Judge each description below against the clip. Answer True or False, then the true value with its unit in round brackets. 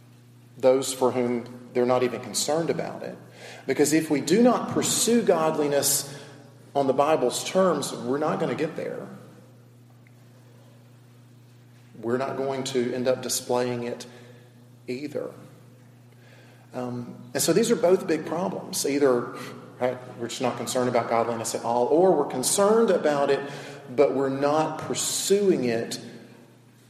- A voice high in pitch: False (125 Hz)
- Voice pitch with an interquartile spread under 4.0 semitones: True (2.6 semitones)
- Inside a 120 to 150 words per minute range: True (140 wpm)